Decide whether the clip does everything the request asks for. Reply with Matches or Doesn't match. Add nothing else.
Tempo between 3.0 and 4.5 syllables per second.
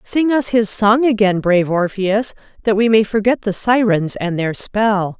Matches